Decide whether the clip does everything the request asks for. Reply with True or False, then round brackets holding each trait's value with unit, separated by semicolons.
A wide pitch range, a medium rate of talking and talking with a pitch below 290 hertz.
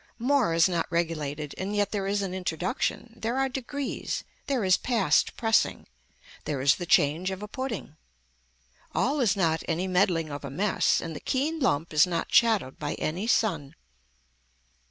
True (5.9 semitones; 170 wpm; 185 Hz)